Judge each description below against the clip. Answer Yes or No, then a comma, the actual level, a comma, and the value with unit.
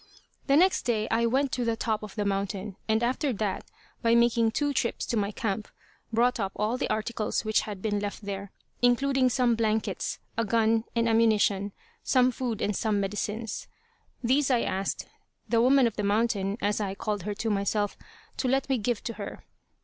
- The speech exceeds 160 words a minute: Yes, average, 190 wpm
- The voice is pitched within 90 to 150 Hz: No, high, 225 Hz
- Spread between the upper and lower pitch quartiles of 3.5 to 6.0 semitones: No, average, 2.7 semitones